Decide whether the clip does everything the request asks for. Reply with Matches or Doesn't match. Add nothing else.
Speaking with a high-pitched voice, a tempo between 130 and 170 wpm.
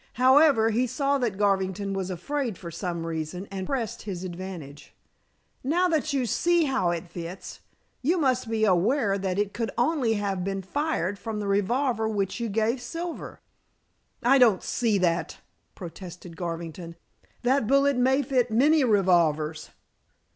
Matches